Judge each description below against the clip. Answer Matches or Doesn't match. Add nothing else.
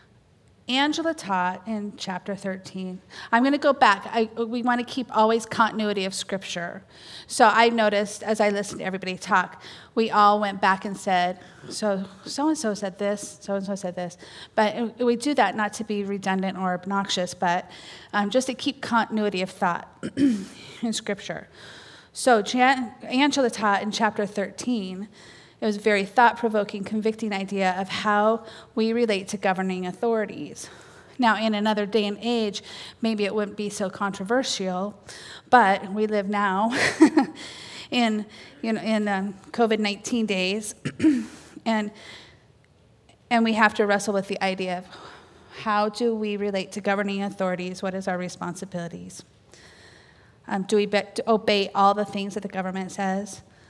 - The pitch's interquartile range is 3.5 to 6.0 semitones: Doesn't match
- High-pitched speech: Matches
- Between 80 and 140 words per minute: Doesn't match